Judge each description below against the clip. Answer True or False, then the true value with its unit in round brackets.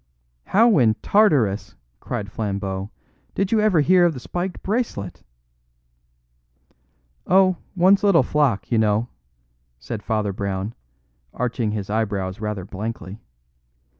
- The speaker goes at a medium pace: False (115 wpm)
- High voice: False (115 Hz)